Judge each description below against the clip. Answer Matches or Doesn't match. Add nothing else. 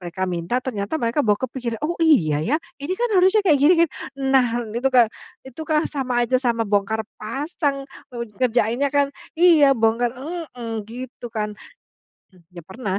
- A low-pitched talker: Doesn't match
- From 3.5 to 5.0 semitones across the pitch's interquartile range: Matches